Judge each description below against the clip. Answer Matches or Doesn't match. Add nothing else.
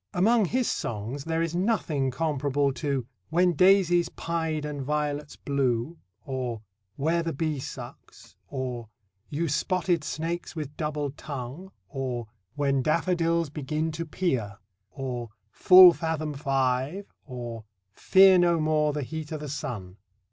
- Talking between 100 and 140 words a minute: Matches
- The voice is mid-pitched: Matches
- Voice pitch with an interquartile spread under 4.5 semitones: Matches